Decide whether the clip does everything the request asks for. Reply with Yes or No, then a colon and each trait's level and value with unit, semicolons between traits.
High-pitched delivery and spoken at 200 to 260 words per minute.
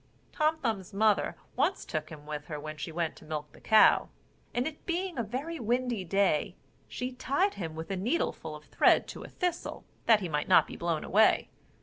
Yes: high, 205 Hz; fast, 205 wpm